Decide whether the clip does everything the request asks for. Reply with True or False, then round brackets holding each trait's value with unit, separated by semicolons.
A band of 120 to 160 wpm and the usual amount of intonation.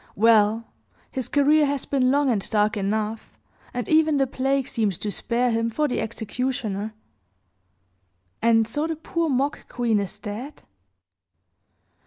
True (140 wpm; 4.2 semitones)